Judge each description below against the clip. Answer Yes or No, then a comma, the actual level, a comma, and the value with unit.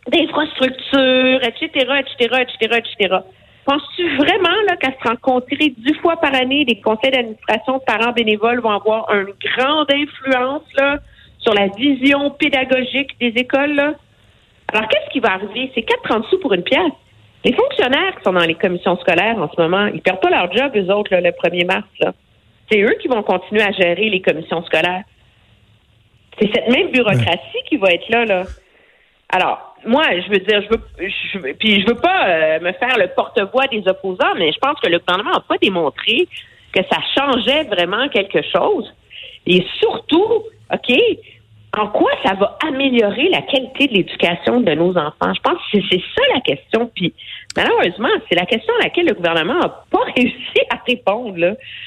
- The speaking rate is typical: Yes, average, 185 wpm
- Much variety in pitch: Yes, wide, 6.5 semitones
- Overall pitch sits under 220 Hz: No, high, 240 Hz